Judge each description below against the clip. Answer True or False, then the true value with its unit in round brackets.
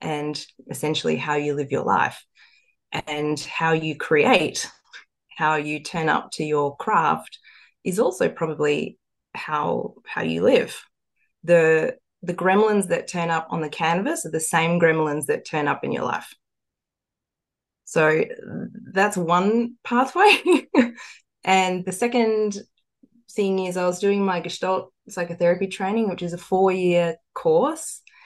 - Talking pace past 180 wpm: False (140 wpm)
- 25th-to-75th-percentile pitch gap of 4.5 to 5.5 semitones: True (5.1 semitones)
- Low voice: False (175 Hz)